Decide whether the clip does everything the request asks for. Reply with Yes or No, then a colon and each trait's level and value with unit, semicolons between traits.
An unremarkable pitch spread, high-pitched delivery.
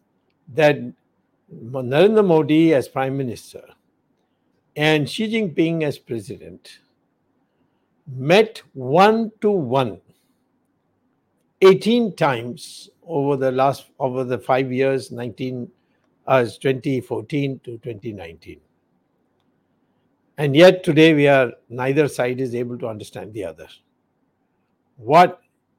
No: average, 4.2 semitones; low, 135 Hz